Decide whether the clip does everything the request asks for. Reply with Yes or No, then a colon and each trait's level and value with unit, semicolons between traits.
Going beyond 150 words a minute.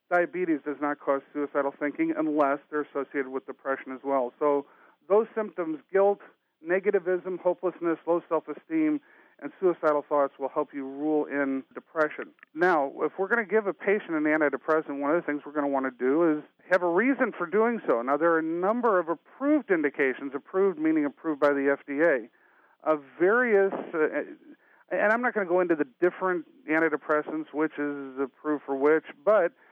Yes: average, 180 wpm